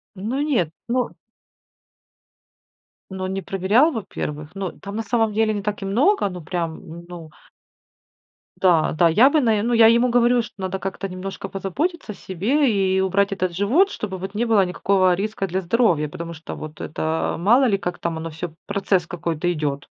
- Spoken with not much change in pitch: No, average, 4.2 semitones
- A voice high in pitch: Yes, high, 195 Hz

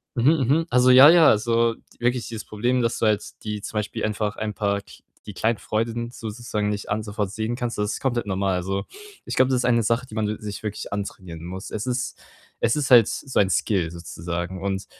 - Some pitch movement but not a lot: Yes, average, 3.0 semitones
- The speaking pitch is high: No, low, 110 Hz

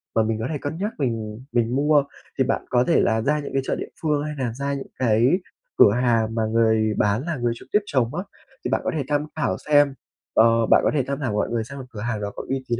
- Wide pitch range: No, average, 4.3 semitones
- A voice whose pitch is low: Yes, low, 125 Hz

